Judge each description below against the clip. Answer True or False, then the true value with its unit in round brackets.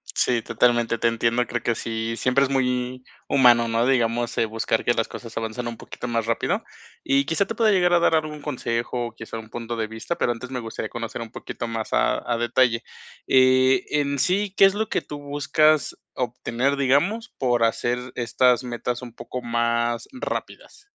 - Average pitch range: True (3.1 semitones)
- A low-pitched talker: True (120 Hz)